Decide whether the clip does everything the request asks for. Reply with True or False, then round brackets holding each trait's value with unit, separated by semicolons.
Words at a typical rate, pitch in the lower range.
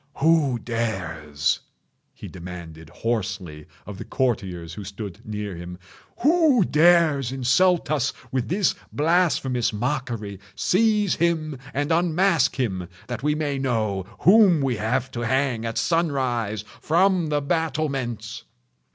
False (115 wpm; 130 Hz)